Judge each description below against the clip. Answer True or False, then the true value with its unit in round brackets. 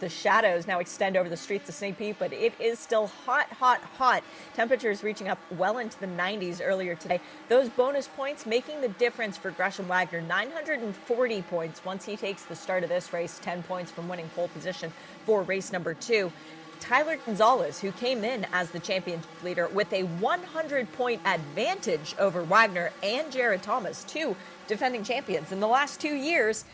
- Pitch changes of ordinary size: False (5.7 semitones)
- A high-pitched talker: True (200 Hz)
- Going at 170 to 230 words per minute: True (185 wpm)